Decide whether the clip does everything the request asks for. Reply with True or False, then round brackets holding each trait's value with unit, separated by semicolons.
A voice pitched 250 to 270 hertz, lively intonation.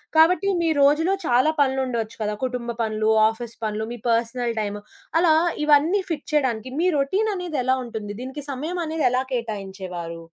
True (255 Hz; 6.0 semitones)